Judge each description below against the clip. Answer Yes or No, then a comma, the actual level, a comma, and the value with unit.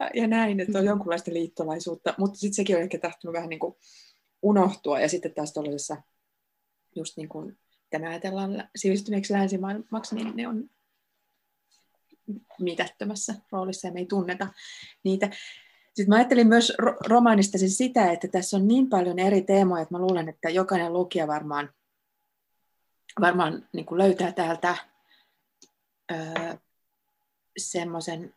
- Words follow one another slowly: No, average, 135 wpm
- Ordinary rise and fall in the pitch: Yes, average, 3.6 semitones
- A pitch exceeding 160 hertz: Yes, high, 190 Hz